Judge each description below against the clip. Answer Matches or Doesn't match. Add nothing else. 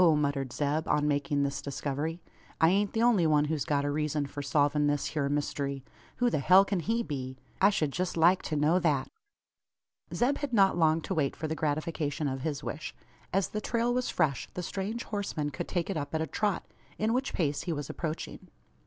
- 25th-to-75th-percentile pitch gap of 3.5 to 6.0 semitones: Matches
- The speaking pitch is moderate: Matches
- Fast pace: Matches